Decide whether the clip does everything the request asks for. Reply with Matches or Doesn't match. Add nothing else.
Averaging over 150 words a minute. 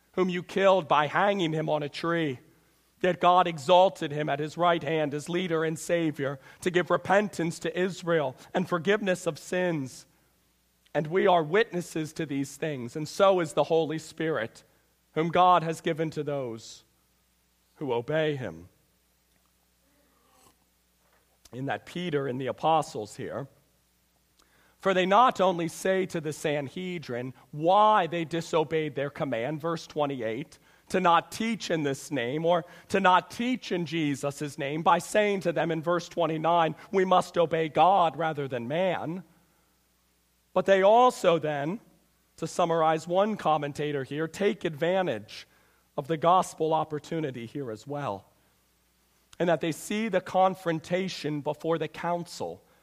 Doesn't match